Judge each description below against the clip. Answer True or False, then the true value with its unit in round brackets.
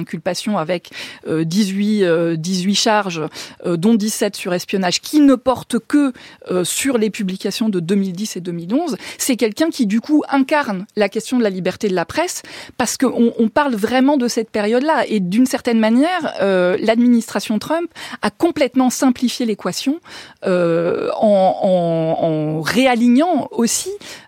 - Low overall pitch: False (220 Hz)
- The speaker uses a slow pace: True (140 wpm)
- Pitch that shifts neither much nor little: False (5.7 semitones)